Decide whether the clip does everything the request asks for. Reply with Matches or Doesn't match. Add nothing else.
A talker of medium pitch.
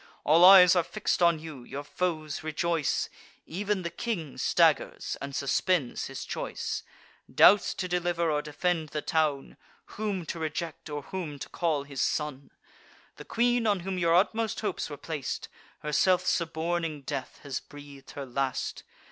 Matches